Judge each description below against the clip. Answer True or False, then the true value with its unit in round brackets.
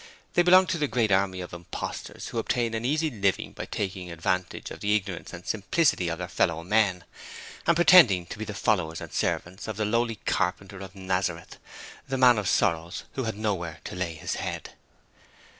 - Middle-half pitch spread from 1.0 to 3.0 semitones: False (4.2 semitones)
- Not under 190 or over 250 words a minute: True (195 wpm)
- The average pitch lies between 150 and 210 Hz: False (100 Hz)